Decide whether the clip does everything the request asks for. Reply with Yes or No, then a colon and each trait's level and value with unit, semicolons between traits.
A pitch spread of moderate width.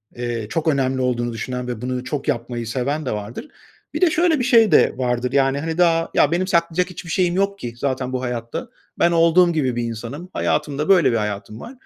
No: wide, 5.9 semitones